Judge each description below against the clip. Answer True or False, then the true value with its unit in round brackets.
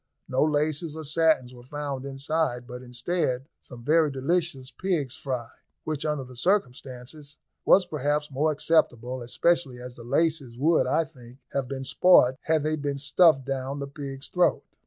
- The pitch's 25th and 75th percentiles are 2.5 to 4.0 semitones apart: True (3.6 semitones)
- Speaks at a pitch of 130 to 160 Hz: True (140 Hz)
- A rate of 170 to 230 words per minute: False (160 wpm)